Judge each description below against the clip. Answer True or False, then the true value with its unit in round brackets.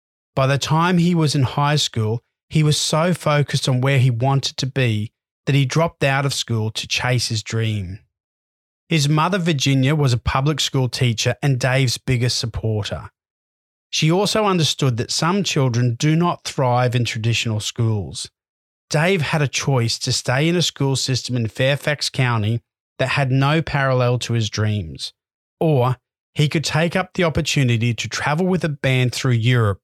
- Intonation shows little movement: False (4.3 semitones)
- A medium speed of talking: True (175 wpm)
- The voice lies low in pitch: True (130 Hz)